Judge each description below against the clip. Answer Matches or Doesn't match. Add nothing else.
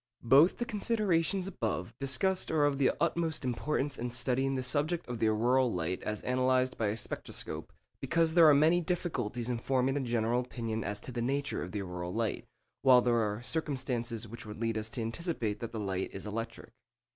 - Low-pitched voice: Matches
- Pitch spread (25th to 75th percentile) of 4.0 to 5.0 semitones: Matches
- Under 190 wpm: Doesn't match